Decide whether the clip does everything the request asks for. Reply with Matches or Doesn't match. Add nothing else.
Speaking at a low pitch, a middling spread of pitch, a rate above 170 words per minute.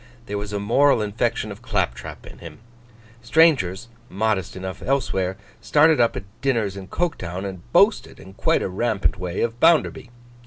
Doesn't match